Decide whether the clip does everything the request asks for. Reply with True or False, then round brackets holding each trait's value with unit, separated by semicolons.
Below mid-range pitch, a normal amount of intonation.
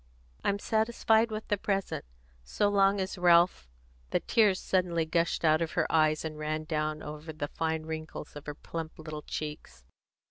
False (160 Hz; 4.1 semitones)